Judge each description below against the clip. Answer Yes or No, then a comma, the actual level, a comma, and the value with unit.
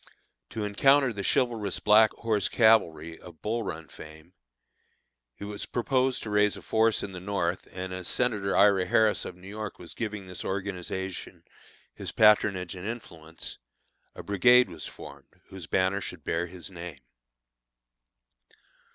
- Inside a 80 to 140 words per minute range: No, average, 150 wpm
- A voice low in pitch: Yes, low, 100 Hz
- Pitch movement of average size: Yes, average, 3.3 semitones